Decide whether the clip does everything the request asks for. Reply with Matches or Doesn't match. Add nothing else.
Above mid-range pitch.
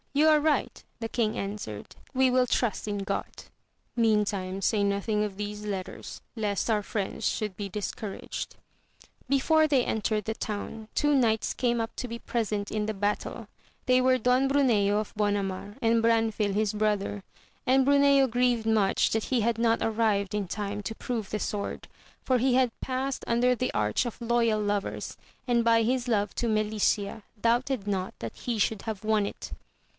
Matches